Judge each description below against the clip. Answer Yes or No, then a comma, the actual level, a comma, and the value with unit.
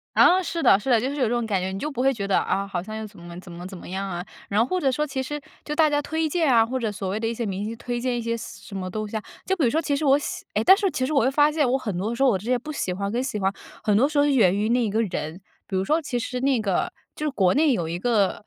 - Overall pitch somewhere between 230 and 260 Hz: Yes, high, 235 Hz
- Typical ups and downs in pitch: No, wide, 5.9 semitones